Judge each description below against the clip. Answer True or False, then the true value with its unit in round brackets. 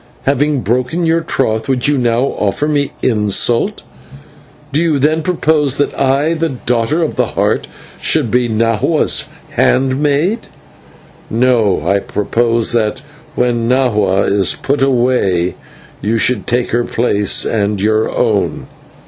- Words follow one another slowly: True (130 wpm)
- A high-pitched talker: False (125 Hz)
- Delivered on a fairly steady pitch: False (4.4 semitones)